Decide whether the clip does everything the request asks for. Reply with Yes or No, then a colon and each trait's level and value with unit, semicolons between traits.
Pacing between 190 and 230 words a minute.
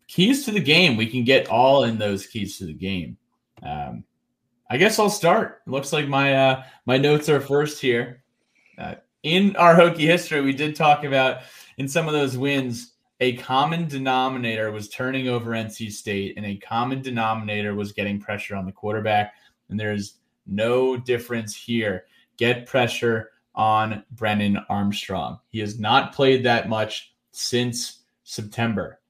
No: average, 165 wpm